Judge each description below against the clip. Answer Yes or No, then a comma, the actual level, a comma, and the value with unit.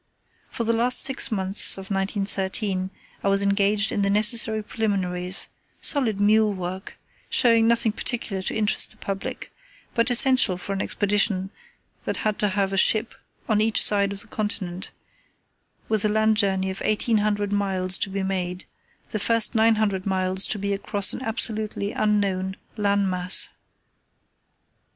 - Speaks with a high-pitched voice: Yes, high, 205 Hz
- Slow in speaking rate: No, average, 155 wpm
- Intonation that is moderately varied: No, narrow, 2.2 semitones